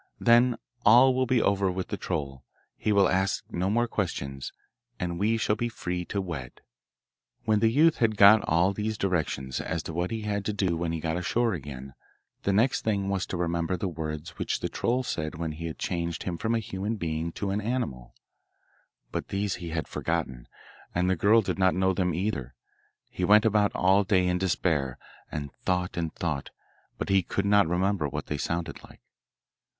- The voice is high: No, very low, 95 Hz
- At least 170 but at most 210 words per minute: Yes, average, 195 wpm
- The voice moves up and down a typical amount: Yes, average, 4.1 semitones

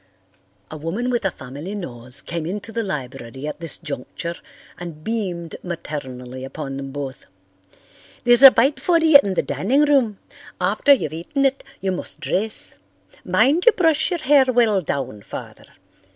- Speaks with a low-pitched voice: No, medium, 185 Hz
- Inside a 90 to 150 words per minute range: No, average, 160 wpm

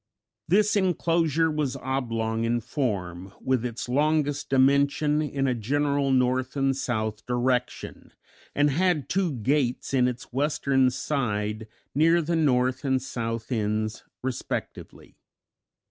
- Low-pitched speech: Yes, low, 130 Hz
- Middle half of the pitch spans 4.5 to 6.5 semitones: No, average, 3.5 semitones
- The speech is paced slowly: Yes, slow, 120 wpm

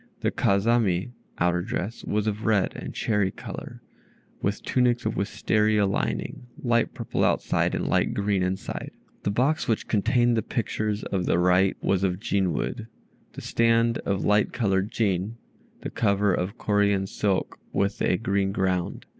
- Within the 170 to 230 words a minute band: No, average, 155 wpm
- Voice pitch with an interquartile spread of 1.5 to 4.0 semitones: Yes, average, 2.9 semitones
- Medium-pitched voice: No, low, 100 Hz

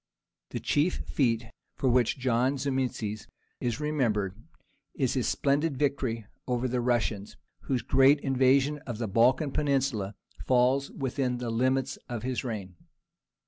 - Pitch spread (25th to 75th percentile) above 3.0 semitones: No, average, 2.7 semitones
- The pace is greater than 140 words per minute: No, slow, 135 wpm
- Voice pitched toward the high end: No, low, 130 Hz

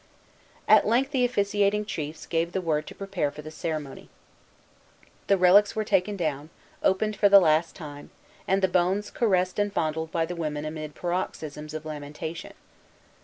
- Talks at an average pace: Yes, average, 165 wpm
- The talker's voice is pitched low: No, medium, 175 Hz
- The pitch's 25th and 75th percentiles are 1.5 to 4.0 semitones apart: No, average, 4.5 semitones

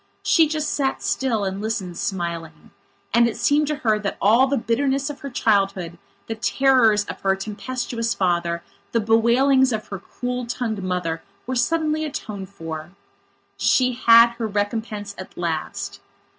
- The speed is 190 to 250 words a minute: No, average, 155 wpm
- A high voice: Yes, high, 225 Hz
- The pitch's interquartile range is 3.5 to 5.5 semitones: Yes, average, 5.0 semitones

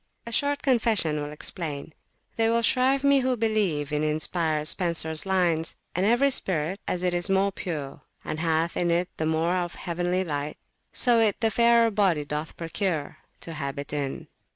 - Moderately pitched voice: Yes, medium, 175 Hz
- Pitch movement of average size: No, wide, 5.9 semitones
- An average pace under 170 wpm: No, average, 175 wpm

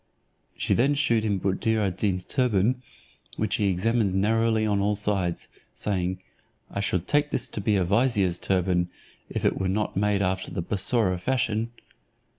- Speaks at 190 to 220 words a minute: No, average, 165 wpm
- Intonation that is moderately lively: Yes, average, 3.3 semitones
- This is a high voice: No, low, 100 Hz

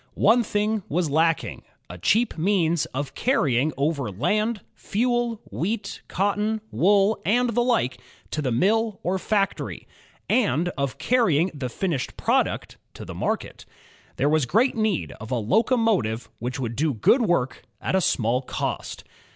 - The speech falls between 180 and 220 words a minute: No, average, 155 wpm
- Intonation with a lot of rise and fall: Yes, wide, 7.9 semitones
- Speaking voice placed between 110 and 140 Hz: No, medium, 180 Hz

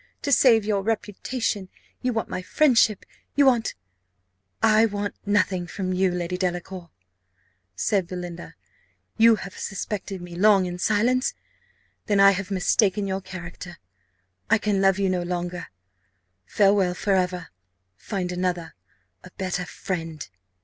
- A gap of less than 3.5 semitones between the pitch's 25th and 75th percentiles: Yes, average, 2.7 semitones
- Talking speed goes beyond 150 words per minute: No, slow, 135 wpm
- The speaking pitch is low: No, high, 190 Hz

